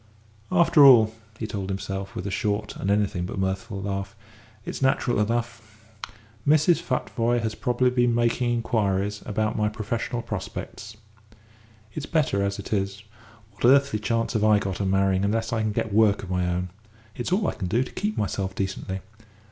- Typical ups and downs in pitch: Yes, average, 3.4 semitones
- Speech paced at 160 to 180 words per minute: Yes, average, 175 wpm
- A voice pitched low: Yes, low, 110 Hz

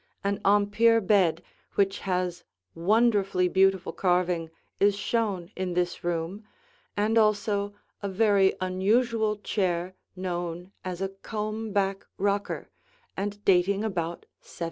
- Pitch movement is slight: Yes, narrow, 2.3 semitones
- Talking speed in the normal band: No, slow, 120 wpm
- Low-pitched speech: No, high, 195 Hz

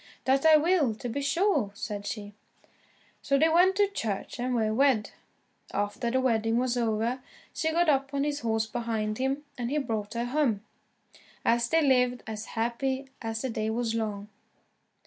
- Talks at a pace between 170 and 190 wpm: Yes, average, 175 wpm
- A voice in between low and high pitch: No, high, 245 Hz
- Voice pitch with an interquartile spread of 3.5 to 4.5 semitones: Yes, average, 3.9 semitones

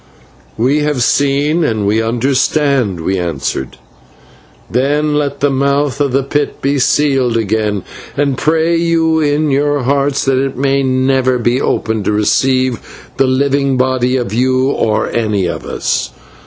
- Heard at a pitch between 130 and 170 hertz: Yes, low, 135 Hz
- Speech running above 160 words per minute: No, average, 155 wpm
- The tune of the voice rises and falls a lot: No, average, 3.1 semitones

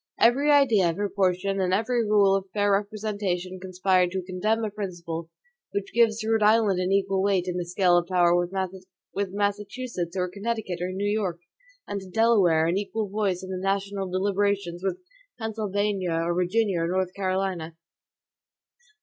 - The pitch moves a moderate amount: No, narrow, 2.3 semitones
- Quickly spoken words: No, average, 165 wpm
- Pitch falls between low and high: No, high, 195 Hz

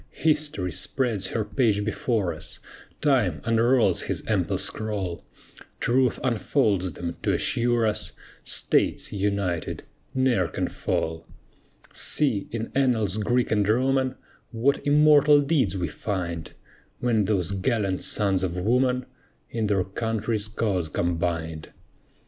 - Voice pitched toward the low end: Yes, low, 110 Hz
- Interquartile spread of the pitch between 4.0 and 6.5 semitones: Yes, average, 5.2 semitones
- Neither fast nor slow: No, slow, 120 wpm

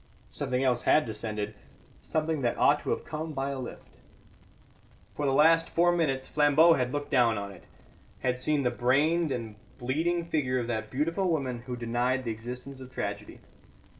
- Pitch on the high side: No, low, 130 Hz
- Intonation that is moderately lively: Yes, average, 4.1 semitones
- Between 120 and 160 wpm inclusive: No, average, 175 wpm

